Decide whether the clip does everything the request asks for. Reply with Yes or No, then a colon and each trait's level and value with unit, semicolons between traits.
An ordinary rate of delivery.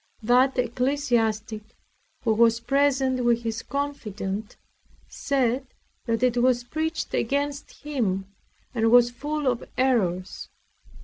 No: slow, 110 wpm